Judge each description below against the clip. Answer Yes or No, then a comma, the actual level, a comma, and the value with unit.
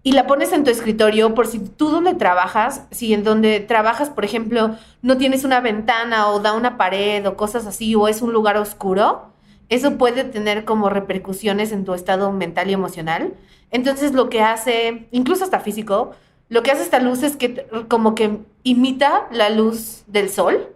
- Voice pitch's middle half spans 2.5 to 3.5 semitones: Yes, average, 3.2 semitones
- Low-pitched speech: No, high, 220 Hz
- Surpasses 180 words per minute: Yes, fast, 190 wpm